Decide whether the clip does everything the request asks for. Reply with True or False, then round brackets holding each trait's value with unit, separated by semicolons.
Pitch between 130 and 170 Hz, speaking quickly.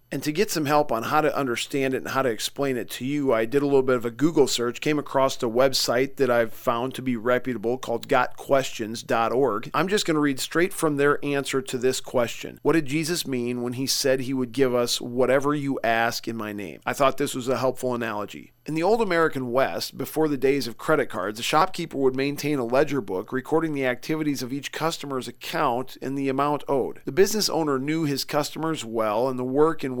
True (135 Hz; 230 wpm)